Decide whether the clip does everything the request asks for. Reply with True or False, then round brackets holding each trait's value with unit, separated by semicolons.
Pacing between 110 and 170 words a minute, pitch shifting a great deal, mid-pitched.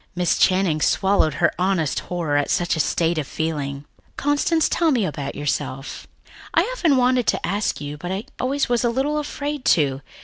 False (180 wpm; 9.0 semitones; 180 Hz)